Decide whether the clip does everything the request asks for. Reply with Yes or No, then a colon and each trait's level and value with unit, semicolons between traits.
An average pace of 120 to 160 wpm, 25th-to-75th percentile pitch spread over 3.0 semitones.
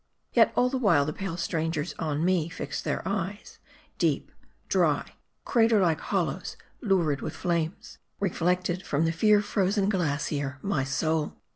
Yes: average, 145 wpm; average, 4.0 semitones